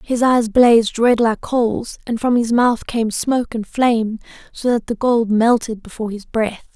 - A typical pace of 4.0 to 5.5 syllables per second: Yes, 4.6 syllables/s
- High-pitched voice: Yes, high, 230 Hz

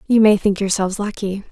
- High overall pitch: Yes, high, 200 Hz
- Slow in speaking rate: No, average, 200 wpm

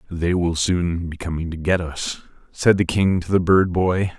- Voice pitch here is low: Yes, very low, 85 Hz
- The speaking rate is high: Yes, fast, 215 wpm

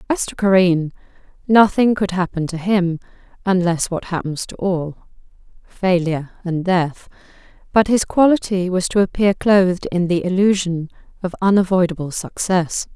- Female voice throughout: Yes, female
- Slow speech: Yes, slow, 130 wpm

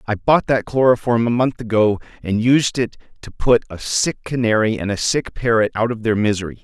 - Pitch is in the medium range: No, low, 115 Hz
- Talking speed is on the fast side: Yes, fast, 210 wpm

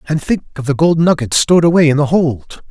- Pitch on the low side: No, medium, 155 Hz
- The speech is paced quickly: Yes, fast, 245 wpm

